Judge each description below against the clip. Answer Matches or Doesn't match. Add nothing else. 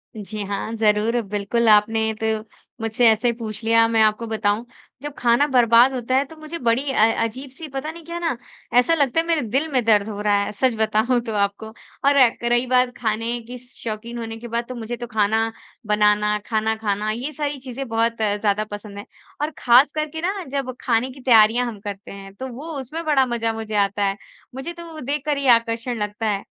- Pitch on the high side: Matches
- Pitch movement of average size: Matches